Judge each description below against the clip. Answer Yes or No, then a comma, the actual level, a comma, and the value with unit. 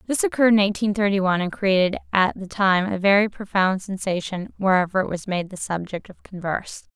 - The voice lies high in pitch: Yes, high, 195 Hz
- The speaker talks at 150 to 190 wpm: No, average, 200 wpm